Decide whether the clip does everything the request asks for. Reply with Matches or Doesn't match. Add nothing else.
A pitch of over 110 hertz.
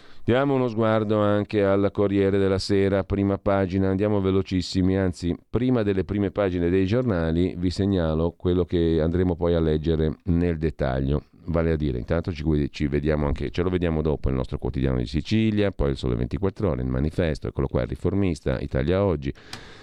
Doesn't match